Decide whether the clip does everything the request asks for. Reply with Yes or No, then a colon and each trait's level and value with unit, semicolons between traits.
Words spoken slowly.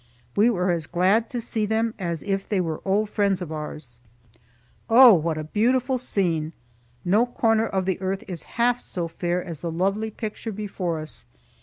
No: average, 180 wpm